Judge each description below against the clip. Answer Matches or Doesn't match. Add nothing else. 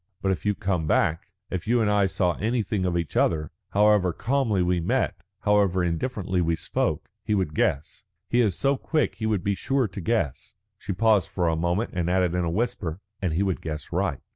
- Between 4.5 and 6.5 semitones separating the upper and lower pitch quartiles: Doesn't match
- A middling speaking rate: Doesn't match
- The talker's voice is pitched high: Doesn't match